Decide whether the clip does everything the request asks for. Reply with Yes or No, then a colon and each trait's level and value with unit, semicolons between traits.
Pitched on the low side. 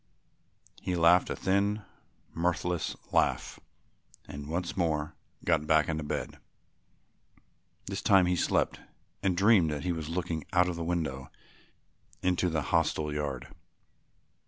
Yes: very low, 85 Hz